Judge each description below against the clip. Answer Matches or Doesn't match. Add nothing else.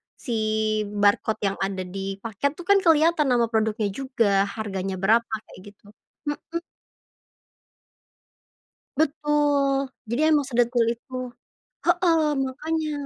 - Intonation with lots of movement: Matches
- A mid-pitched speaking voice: Doesn't match